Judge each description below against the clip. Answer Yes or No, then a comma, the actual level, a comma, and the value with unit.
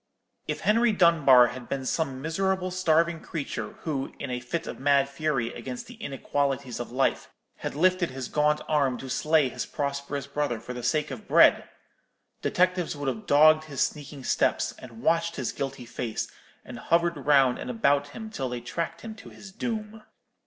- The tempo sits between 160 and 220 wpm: Yes, average, 175 wpm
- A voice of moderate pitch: Yes, medium, 145 Hz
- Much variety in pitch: No, average, 4.3 semitones